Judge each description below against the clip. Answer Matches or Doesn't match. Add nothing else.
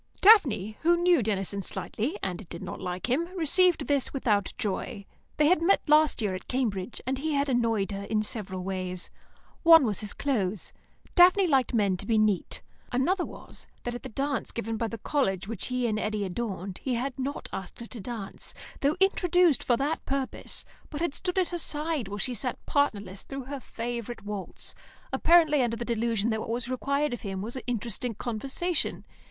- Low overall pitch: Doesn't match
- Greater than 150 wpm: Matches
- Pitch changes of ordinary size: Doesn't match